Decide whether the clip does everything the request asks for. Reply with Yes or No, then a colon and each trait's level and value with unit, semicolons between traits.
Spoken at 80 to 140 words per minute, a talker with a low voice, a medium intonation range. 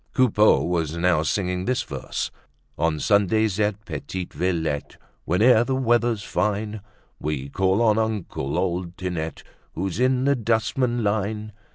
Yes: slow, 135 wpm; low, 100 Hz; average, 4.1 semitones